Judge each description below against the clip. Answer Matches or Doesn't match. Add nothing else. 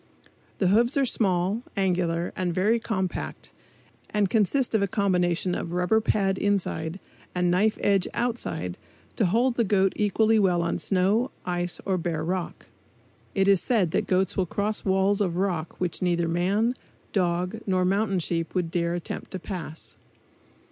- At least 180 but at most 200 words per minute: Doesn't match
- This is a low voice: Doesn't match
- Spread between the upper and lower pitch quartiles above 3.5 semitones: Doesn't match